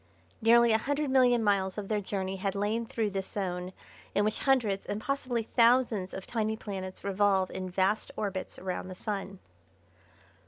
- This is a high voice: Yes, high, 205 Hz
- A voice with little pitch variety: No, average, 3.2 semitones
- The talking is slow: No, average, 165 wpm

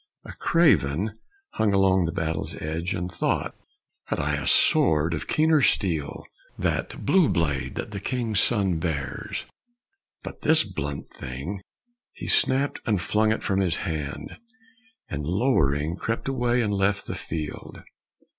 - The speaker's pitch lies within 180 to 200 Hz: No, very low, 95 Hz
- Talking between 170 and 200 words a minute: No, average, 145 wpm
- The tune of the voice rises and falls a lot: Yes, wide, 6.5 semitones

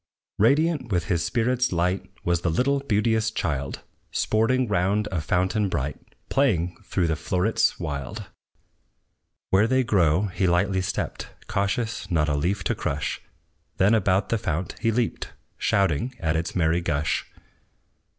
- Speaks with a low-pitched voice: Yes, very low, 95 Hz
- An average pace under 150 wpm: Yes, average, 140 wpm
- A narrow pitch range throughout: No, average, 4.8 semitones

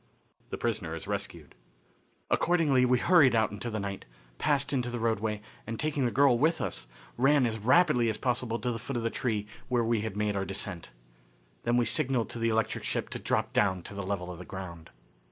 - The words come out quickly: Yes, fast, 210 wpm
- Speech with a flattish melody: No, average, 3.8 semitones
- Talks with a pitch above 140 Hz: No, low, 115 Hz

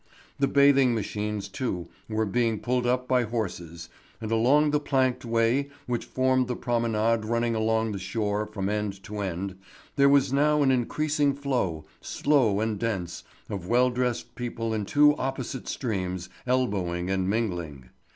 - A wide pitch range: No, average, 4.1 semitones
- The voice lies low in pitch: Yes, low, 115 Hz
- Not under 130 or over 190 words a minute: Yes, average, 155 wpm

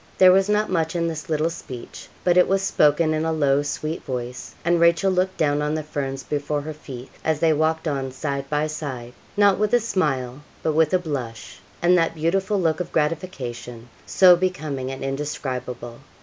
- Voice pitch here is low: No, medium, 155 Hz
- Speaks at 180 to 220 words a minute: Yes, average, 190 wpm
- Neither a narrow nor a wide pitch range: Yes, average, 4.1 semitones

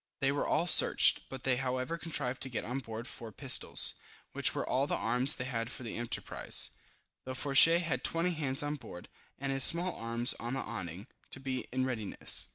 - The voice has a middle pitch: No, low, 130 Hz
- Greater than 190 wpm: Yes, average, 200 wpm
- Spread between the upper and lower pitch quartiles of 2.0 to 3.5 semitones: Yes, average, 2.8 semitones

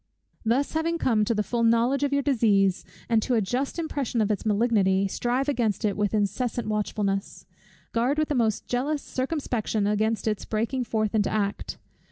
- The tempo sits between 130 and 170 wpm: No, average, 180 wpm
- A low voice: No, high, 230 Hz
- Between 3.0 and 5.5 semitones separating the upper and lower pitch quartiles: Yes, average, 3.7 semitones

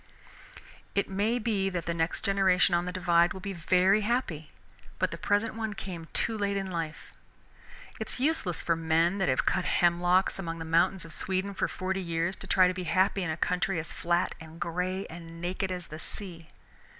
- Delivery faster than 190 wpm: Yes, average, 200 wpm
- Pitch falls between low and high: Yes, medium, 180 Hz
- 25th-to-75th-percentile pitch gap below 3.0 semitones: Yes, narrow, 2.5 semitones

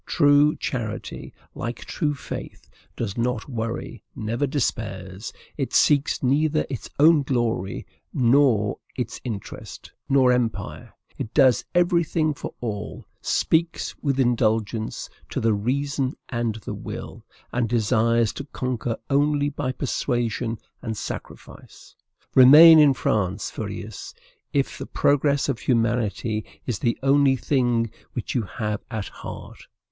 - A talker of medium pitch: No, low, 125 Hz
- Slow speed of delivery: Yes, slow, 125 wpm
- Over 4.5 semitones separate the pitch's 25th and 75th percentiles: No, average, 4.0 semitones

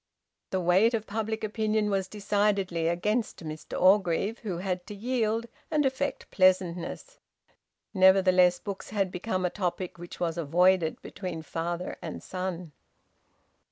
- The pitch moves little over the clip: No, average, 3.1 semitones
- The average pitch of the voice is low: No, high, 190 Hz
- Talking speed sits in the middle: No, slow, 130 wpm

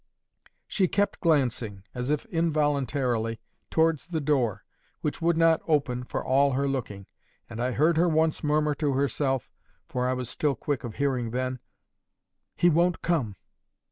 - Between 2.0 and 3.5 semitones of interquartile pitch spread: No, average, 4.1 semitones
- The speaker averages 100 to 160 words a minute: Yes, average, 145 wpm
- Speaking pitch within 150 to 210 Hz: No, medium, 140 Hz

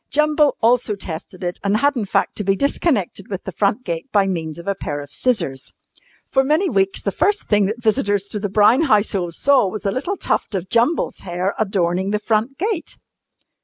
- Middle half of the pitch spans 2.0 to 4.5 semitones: No, average, 5.1 semitones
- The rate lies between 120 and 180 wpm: No, average, 200 wpm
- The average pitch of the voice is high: Yes, high, 205 Hz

